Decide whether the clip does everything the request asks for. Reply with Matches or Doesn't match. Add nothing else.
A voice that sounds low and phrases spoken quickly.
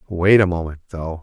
Doesn't match